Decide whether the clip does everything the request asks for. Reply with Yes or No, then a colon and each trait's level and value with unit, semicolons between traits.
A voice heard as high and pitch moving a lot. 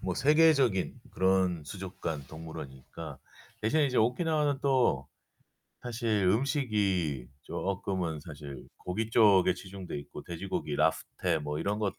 No: very low, 95 Hz; wide, 6.6 semitones